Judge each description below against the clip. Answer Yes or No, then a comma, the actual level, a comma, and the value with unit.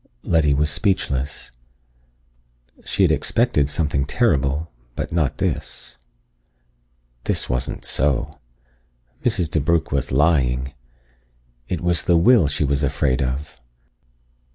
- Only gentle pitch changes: No, average, 3.5 semitones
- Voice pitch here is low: Yes, very low, 75 Hz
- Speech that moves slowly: Yes, slow, 105 wpm